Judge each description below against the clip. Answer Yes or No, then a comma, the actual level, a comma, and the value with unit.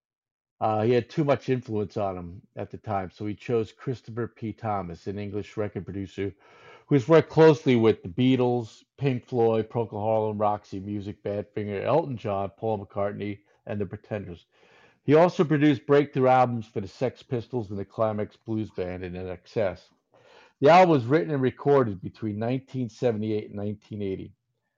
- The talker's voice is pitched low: Yes, low, 110 Hz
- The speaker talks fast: No, average, 165 wpm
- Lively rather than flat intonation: No, average, 3.7 semitones